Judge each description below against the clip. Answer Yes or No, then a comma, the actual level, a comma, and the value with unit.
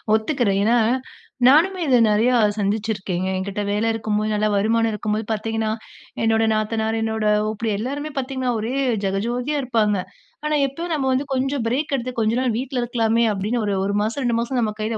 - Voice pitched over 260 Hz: No, high, 225 Hz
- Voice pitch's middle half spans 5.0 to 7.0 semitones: No, average, 3.1 semitones